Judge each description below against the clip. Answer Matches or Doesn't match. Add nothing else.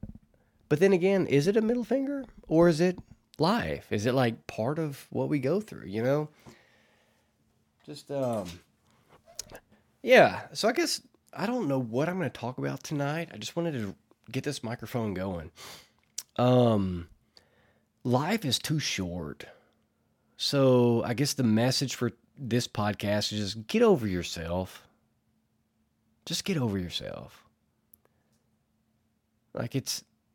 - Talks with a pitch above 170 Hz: Doesn't match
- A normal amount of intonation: Doesn't match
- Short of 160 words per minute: Matches